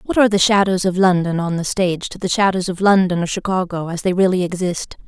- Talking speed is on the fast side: Yes, fast, 235 wpm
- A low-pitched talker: No, medium, 185 Hz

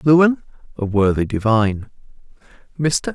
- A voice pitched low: Yes, low, 130 Hz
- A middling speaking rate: No, slow, 95 wpm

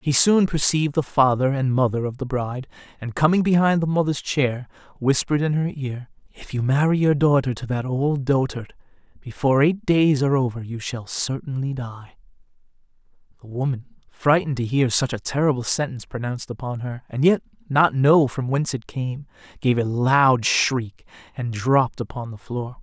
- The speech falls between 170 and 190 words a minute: Yes, average, 175 wpm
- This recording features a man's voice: Yes, male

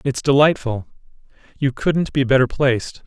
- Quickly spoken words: No, slow, 135 wpm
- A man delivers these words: Yes, male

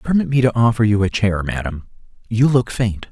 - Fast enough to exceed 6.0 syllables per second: No, 5.4 syllables/s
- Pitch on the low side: Yes, low, 110 Hz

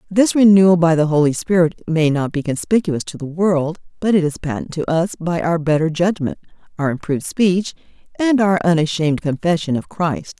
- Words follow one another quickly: No, average, 185 wpm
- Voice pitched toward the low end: No, medium, 170 Hz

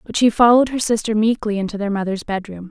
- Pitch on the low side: No, high, 215 Hz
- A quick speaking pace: Yes, fast, 220 wpm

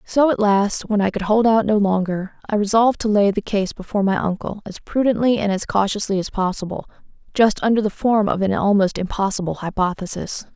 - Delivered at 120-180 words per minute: No, average, 200 wpm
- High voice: Yes, high, 205 Hz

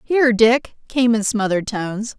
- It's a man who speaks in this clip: No, female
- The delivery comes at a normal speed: Yes, average, 165 wpm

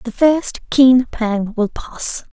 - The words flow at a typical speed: Yes, average, 155 wpm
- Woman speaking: Yes, female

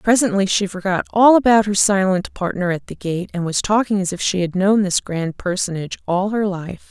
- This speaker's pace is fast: Yes, fast, 215 wpm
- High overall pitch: Yes, high, 195 Hz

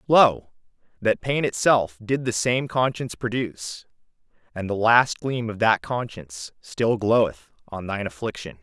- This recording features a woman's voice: No, male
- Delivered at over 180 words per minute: No, average, 145 wpm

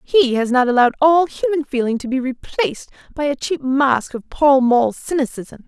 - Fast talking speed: No, average, 190 wpm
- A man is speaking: No, female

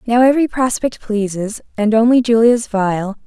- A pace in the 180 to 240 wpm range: No, average, 145 wpm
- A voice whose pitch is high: Yes, high, 225 Hz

